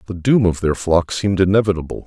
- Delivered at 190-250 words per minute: Yes, fast, 205 wpm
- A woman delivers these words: No, male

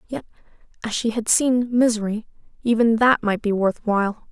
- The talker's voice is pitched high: Yes, high, 225 Hz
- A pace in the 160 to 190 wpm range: Yes, average, 165 wpm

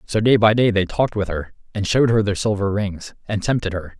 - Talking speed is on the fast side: Yes, fast, 255 wpm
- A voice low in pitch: Yes, low, 105 Hz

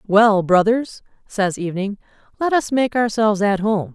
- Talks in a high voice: Yes, high, 210 Hz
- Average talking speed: Yes, average, 150 wpm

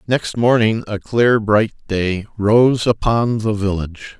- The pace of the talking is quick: No, average, 145 wpm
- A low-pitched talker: Yes, low, 110 Hz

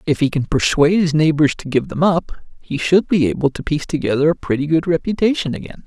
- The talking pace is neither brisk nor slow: No, fast, 225 wpm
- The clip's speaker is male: Yes, male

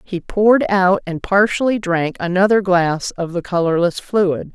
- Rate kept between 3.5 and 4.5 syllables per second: Yes, 4.4 syllables/s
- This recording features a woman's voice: Yes, female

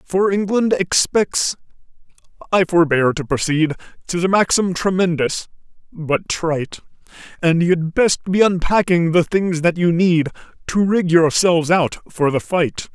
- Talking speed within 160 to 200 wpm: No, slow, 135 wpm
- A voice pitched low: No, medium, 175 Hz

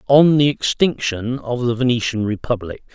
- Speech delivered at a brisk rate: No, average, 145 wpm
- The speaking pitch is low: Yes, low, 125 Hz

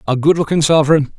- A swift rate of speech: No, average, 150 wpm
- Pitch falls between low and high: Yes, medium, 150 Hz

